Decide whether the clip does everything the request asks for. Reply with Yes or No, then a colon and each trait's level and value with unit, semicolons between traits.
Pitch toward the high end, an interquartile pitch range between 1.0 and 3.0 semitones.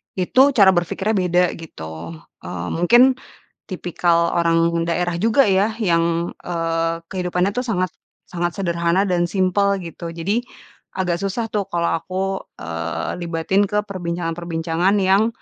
No: medium, 175 Hz; average, 2.7 semitones